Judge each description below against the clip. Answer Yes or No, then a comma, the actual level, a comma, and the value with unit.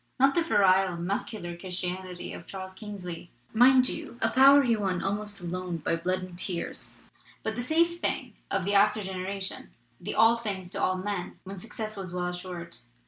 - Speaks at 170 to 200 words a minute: Yes, average, 185 wpm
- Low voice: No, high, 190 Hz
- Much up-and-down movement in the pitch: No, average, 3.2 semitones